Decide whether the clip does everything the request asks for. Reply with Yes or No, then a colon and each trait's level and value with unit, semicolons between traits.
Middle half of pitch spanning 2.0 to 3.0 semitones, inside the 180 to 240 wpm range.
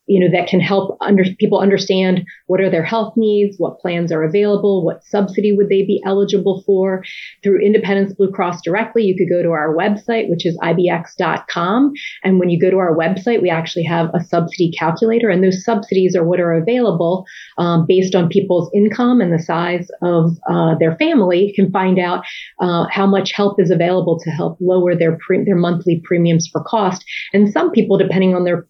Yes: narrow, 2.6 semitones; average, 200 wpm